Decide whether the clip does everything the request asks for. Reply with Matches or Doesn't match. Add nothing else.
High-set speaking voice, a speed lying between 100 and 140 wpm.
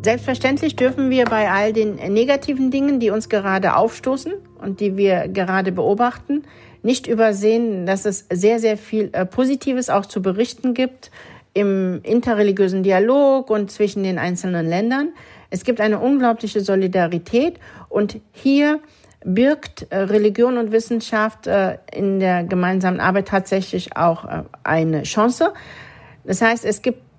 Matches